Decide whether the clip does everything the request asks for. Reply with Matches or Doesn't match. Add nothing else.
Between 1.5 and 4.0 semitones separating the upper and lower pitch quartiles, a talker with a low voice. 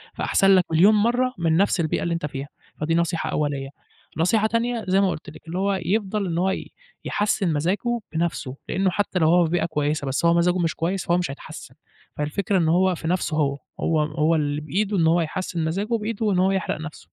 Doesn't match